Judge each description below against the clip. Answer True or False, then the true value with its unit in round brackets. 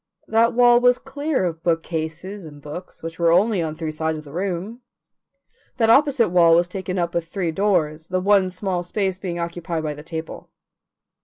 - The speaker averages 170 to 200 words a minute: True (185 wpm)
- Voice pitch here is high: False (175 Hz)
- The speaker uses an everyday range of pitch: True (3.9 semitones)